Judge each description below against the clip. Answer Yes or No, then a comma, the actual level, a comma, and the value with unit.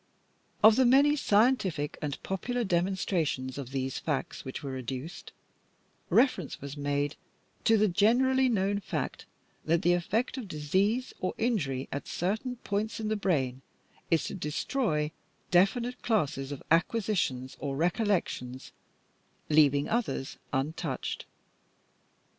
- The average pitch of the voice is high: No, medium, 175 Hz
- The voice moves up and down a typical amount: No, wide, 7.4 semitones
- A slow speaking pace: Yes, slow, 125 wpm